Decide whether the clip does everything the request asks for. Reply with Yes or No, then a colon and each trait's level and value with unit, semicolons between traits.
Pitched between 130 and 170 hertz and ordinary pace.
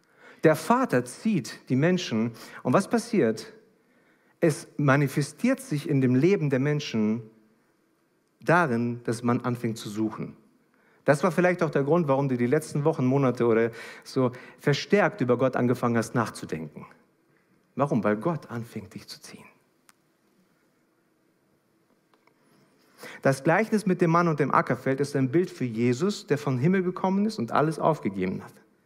Yes: medium, 140 Hz; average, 150 wpm